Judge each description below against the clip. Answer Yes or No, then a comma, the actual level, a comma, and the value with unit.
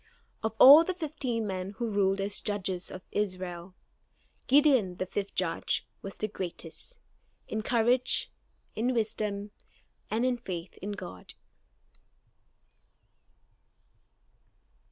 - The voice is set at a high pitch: Yes, high, 205 Hz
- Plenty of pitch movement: No, average, 4.4 semitones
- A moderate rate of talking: No, slow, 110 wpm